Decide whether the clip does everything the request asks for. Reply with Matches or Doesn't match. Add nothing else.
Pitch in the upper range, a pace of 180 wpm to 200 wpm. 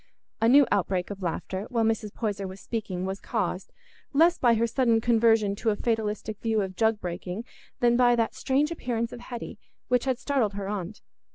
Matches